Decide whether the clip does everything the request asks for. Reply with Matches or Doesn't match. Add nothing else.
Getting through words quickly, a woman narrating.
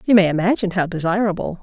Doesn't match